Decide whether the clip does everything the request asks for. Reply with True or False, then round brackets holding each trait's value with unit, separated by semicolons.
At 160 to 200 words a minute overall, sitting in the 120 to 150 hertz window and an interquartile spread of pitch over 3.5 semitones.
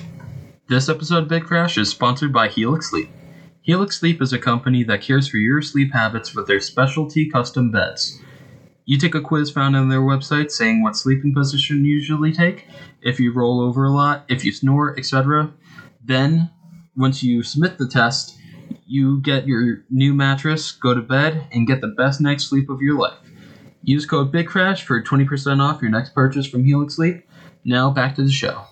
False (190 wpm; 140 Hz; 3.2 semitones)